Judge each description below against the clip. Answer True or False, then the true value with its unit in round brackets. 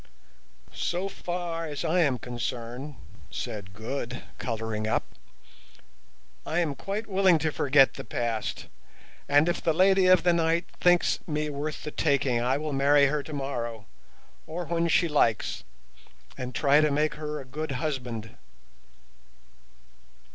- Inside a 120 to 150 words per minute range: True (140 wpm)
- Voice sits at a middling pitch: True (150 Hz)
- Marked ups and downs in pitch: False (4.9 semitones)